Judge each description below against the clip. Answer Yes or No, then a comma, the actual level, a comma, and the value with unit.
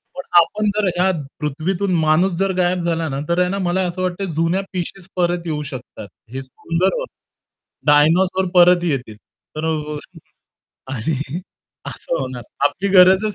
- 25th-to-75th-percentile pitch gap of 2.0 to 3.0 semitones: No, average, 3.6 semitones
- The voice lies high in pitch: No, medium, 175 Hz